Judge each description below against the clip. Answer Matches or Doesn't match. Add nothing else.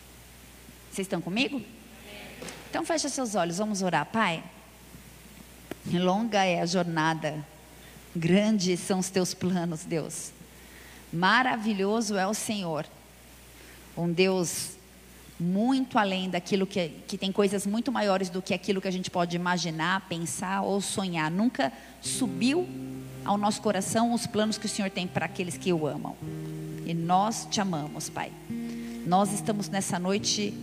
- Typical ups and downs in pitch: Matches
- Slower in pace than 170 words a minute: Matches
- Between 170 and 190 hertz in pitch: Matches